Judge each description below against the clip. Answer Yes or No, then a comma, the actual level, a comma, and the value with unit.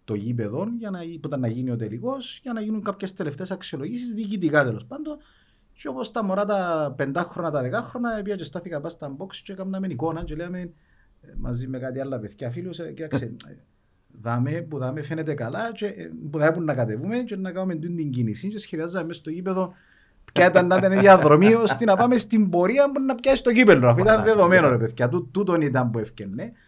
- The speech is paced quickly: Yes, fast, 200 wpm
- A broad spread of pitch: Yes, wide, 6.4 semitones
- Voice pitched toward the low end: No, medium, 175 Hz